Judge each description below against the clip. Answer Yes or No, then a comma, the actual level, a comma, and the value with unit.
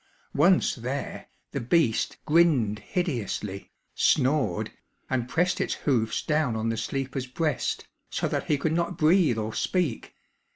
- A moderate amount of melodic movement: No, wide, 6.2 semitones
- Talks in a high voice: No, low, 135 Hz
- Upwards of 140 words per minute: No, slow, 135 wpm